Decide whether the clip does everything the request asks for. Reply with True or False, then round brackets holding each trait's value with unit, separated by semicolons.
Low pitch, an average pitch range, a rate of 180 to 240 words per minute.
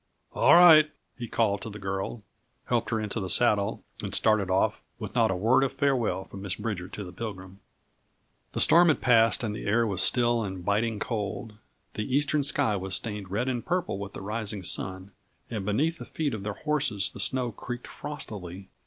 True (110 Hz; 4.0 semitones; 195 wpm)